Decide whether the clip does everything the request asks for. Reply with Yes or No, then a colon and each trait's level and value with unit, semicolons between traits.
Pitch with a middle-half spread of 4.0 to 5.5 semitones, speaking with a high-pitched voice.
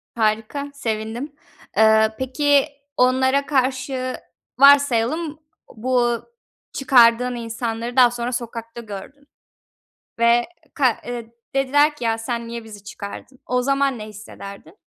No: average, 3.1 semitones; high, 245 Hz